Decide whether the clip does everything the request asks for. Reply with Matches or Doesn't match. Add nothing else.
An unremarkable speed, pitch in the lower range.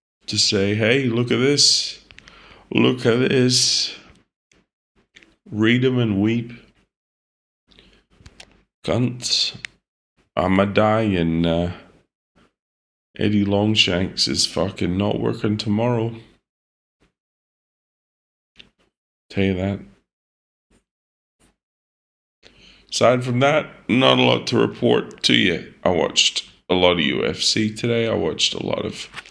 Doesn't match